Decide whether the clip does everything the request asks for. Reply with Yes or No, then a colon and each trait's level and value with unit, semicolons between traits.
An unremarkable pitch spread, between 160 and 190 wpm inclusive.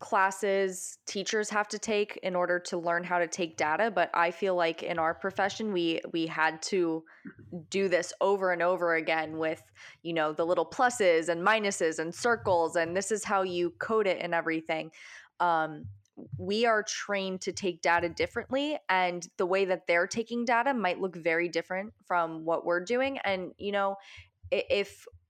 Yes: average, 3.0 semitones; average, 180 wpm